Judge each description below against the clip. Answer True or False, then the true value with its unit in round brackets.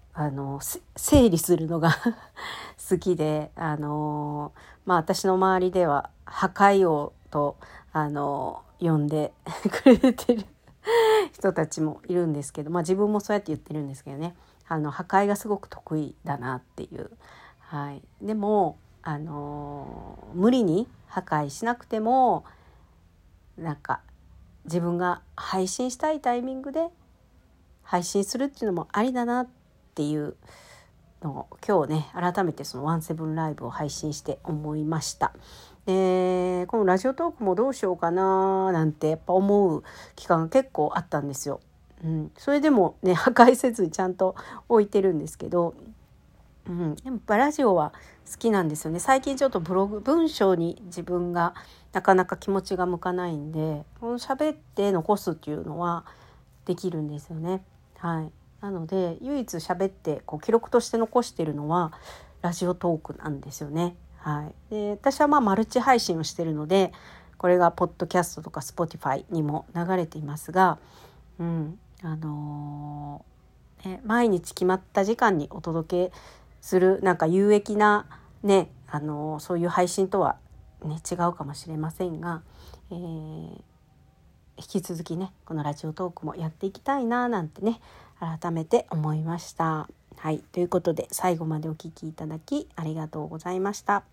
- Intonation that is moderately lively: True (4.3 semitones)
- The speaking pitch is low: False (175 Hz)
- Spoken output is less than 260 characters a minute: False (315 characters per minute)